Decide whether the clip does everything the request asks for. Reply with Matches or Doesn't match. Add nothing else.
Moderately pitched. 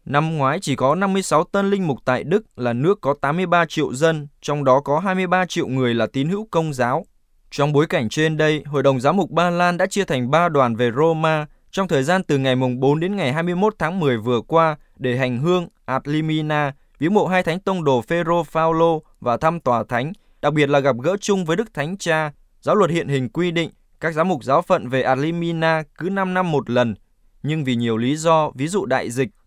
Matches